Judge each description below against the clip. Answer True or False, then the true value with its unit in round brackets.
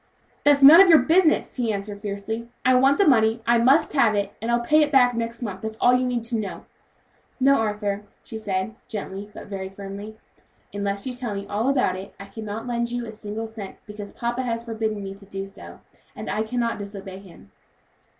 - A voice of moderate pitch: False (220 Hz)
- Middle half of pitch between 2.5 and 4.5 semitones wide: True (3.3 semitones)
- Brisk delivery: True (215 wpm)